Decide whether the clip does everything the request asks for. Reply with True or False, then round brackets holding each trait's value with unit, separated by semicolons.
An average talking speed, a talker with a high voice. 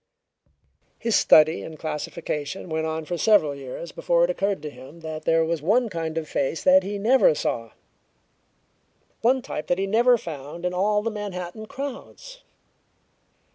False (160 wpm; 175 Hz)